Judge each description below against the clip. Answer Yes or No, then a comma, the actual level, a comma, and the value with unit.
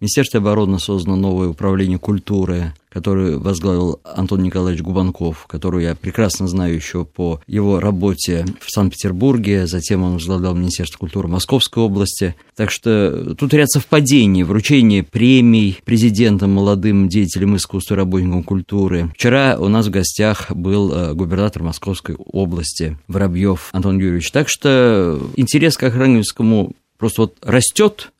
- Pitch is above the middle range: No, very low, 95 Hz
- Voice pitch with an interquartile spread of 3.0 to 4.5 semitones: Yes, average, 3.3 semitones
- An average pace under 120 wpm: No, average, 130 wpm